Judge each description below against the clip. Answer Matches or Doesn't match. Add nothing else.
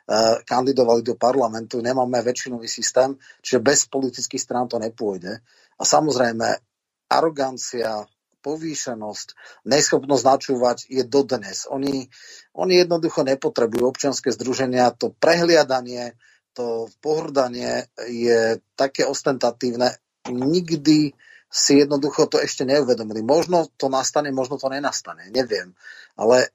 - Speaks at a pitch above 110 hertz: Matches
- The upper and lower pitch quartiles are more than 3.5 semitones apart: Doesn't match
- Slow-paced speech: Matches